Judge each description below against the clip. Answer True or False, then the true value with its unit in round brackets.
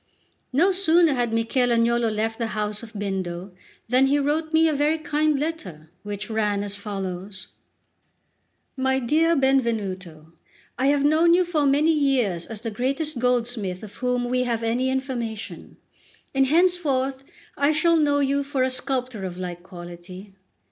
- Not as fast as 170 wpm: True (155 wpm)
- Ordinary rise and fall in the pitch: False (5.7 semitones)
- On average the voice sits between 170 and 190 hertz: False (250 Hz)